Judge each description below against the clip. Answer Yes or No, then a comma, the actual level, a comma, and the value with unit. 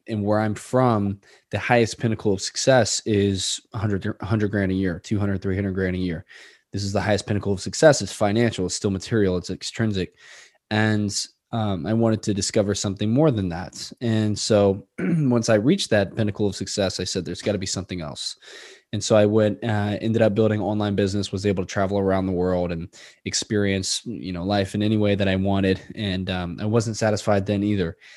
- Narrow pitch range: Yes, narrow, 2.1 semitones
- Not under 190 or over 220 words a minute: Yes, fast, 205 wpm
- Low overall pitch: Yes, low, 100 Hz